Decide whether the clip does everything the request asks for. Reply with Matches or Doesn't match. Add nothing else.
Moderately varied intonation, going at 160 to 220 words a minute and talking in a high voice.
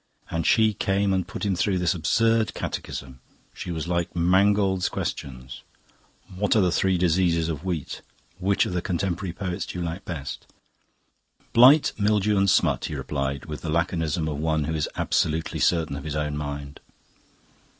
Doesn't match